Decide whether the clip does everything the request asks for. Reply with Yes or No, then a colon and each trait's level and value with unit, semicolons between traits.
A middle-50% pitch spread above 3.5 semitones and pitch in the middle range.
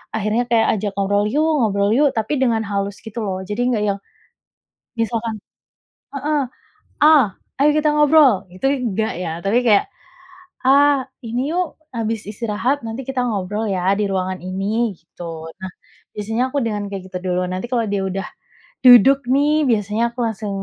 No: average, 4.3 semitones; high, 220 Hz